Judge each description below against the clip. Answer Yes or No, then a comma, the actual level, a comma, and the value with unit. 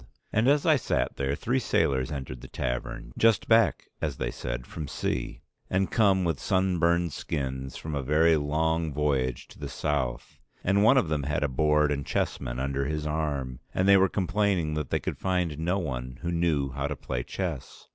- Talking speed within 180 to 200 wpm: Yes, average, 195 wpm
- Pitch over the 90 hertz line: No, very low, 75 Hz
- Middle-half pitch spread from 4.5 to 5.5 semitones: Yes, average, 5.2 semitones